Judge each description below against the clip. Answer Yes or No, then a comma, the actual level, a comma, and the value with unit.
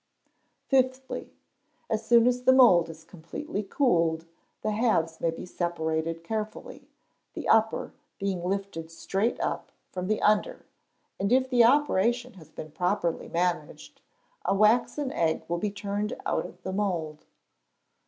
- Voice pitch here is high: Yes, high, 200 Hz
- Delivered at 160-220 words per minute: No, average, 140 wpm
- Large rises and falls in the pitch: Yes, wide, 5.8 semitones